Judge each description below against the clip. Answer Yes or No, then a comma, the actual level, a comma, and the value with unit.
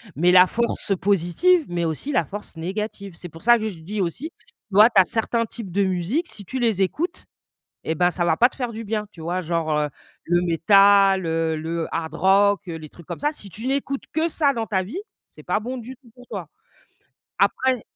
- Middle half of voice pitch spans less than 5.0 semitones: No, wide, 5.5 semitones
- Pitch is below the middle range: No, high, 200 Hz